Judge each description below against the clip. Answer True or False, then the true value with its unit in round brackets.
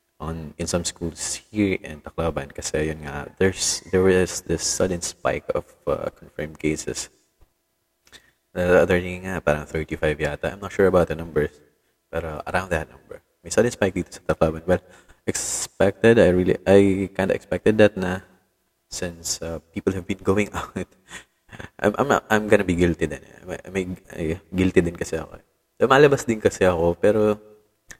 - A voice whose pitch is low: True (90 Hz)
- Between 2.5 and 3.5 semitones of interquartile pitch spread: True (3.0 semitones)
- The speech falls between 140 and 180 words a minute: True (150 wpm)